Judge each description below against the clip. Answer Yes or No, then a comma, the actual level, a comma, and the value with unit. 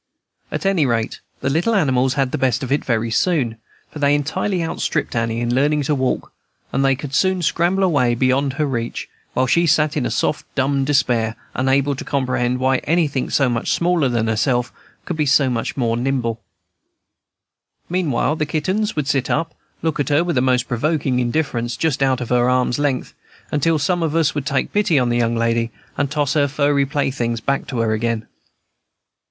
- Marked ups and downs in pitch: No, average, 3.6 semitones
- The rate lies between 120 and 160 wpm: No, average, 195 wpm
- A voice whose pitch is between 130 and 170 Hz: Yes, low, 135 Hz